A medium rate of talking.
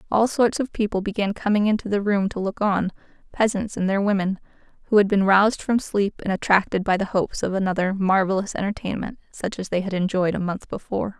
No: fast, 210 wpm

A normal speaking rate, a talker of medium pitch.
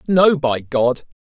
Yes: average, 145 wpm; medium, 145 Hz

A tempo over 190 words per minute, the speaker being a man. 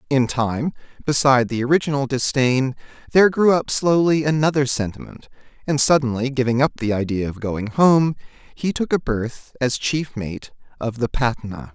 No: average, 160 wpm; male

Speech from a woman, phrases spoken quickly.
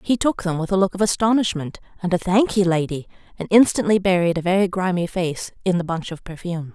Yes: female; fast, 220 wpm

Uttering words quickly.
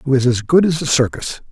Yes: fast, 280 wpm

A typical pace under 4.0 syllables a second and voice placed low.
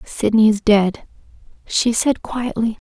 No: 3.8 syllables/s; high, 220 Hz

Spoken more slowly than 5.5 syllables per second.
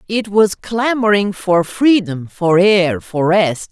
Yes: 3.4 syllables/s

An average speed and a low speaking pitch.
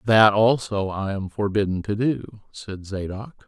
Yes: average, 155 wpm; low, 105 Hz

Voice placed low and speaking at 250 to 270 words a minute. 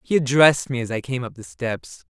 Yes: low, 125 Hz; fast, 255 wpm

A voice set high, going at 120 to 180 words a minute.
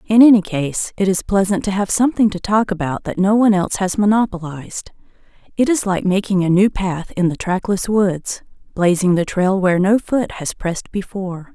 No: high, 195 Hz; average, 195 wpm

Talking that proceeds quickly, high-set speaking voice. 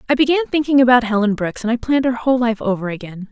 Yes: fast, 255 wpm; high, 240 Hz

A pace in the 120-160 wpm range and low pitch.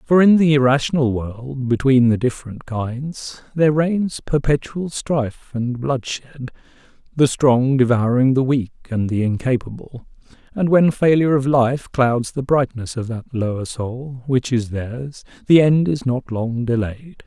Yes: average, 155 wpm; low, 130 Hz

